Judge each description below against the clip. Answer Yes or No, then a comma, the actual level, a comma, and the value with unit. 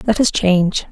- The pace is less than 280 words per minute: Yes, average, 200 wpm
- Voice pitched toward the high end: Yes, high, 195 Hz